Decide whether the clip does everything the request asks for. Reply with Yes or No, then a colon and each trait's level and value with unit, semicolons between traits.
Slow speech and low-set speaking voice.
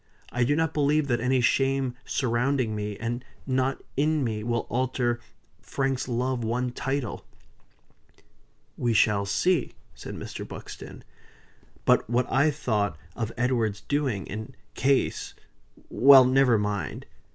Yes: slow, 130 wpm; low, 125 Hz